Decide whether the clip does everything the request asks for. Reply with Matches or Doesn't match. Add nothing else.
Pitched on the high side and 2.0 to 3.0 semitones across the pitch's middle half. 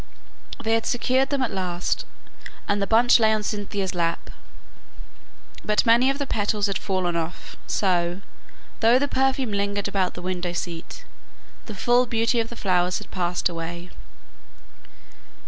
Doesn't match